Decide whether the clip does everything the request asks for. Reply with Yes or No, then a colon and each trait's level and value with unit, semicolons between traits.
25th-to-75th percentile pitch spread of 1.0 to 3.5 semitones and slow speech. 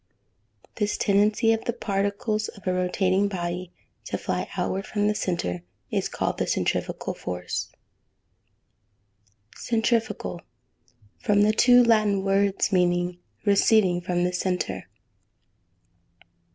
Yes: average, 2.9 semitones; slow, 110 wpm